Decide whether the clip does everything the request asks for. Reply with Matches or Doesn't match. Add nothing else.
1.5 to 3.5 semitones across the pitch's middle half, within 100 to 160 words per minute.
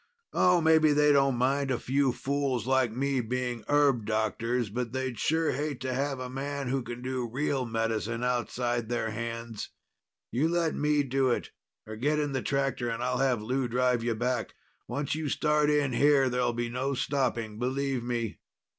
Doesn't match